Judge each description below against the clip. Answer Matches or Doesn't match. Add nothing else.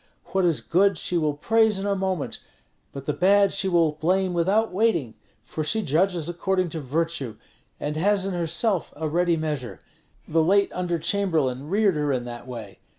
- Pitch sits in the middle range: Matches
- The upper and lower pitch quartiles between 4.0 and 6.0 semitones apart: Matches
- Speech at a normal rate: Matches